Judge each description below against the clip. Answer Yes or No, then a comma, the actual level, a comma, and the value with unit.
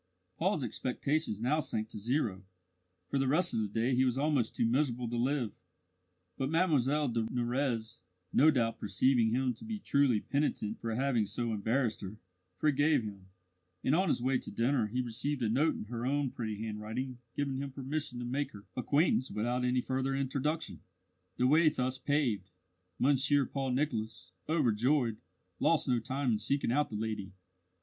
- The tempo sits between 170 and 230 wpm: Yes, average, 175 wpm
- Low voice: Yes, low, 130 Hz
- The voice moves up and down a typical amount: Yes, average, 3.9 semitones